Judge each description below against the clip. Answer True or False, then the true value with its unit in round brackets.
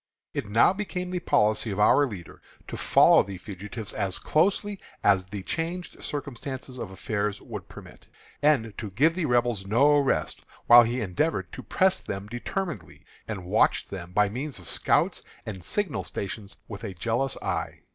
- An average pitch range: False (6.8 semitones)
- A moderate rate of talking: True (165 wpm)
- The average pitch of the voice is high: False (115 Hz)